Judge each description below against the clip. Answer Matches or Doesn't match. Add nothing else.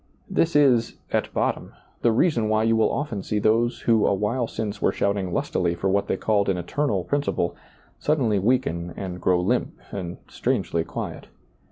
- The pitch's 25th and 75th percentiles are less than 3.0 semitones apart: Doesn't match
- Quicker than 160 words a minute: Matches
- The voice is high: Doesn't match